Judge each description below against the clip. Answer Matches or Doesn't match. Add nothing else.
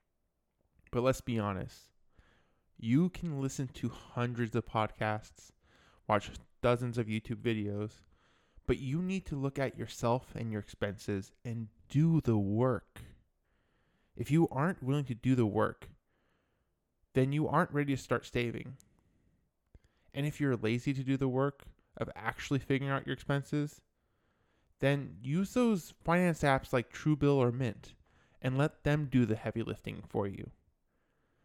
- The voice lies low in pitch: Matches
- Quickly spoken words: Doesn't match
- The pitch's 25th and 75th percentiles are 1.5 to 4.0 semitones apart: Doesn't match